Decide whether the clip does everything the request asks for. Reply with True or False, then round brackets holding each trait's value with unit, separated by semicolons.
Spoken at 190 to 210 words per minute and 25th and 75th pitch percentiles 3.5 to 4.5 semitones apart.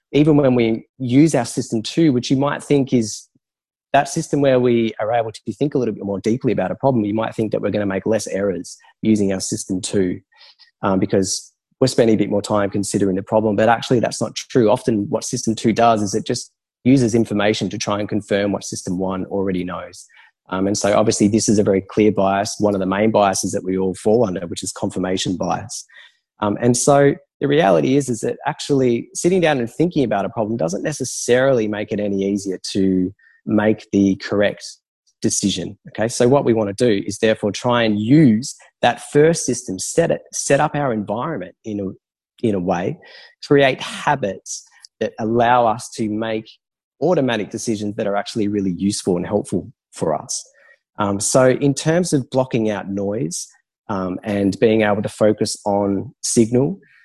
True (200 wpm; 3.9 semitones)